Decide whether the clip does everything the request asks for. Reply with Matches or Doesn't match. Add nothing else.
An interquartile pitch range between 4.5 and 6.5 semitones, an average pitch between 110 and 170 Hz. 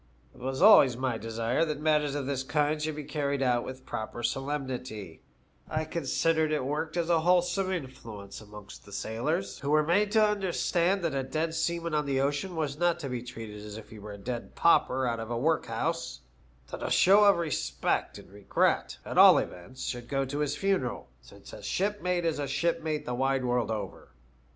Matches